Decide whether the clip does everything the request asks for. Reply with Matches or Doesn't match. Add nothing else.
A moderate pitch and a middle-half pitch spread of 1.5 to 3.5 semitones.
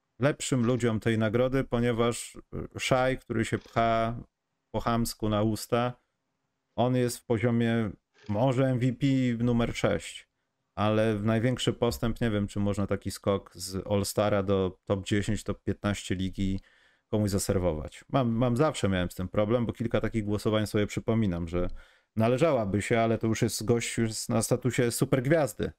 Doesn't match